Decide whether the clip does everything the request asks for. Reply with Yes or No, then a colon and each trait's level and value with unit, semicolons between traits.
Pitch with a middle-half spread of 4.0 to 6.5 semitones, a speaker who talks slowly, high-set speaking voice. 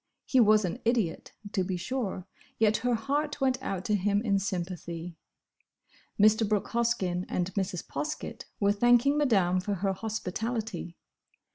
No: average, 4.4 semitones; average, 145 wpm; high, 210 Hz